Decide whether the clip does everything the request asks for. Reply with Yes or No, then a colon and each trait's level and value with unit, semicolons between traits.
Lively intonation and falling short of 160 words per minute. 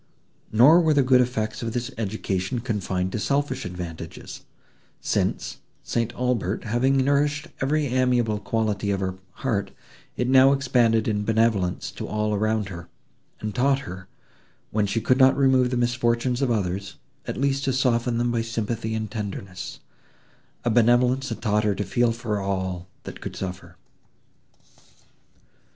No: average, 3.7 semitones; average, 150 wpm